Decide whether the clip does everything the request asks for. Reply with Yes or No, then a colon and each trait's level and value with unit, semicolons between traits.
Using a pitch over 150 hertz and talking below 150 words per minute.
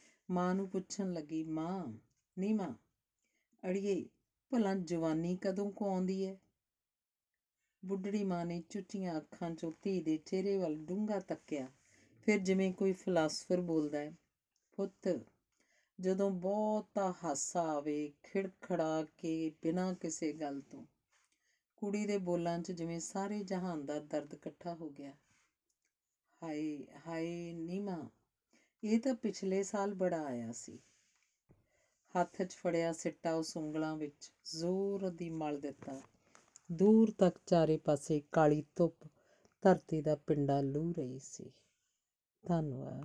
Yes: medium, 170 Hz; average, 125 wpm